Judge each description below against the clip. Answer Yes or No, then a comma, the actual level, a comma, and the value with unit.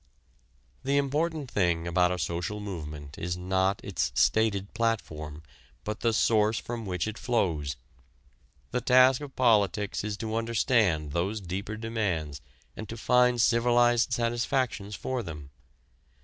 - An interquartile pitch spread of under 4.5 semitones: No, average, 5.1 semitones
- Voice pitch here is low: Yes, low, 105 Hz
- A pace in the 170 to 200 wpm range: No, slow, 135 wpm